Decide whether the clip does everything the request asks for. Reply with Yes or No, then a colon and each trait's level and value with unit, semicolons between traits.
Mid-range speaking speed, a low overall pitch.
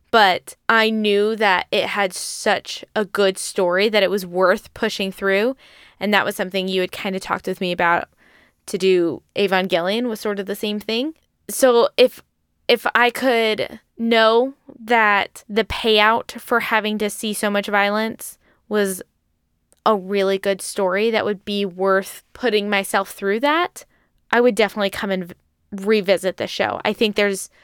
No: average, 170 wpm; high, 205 Hz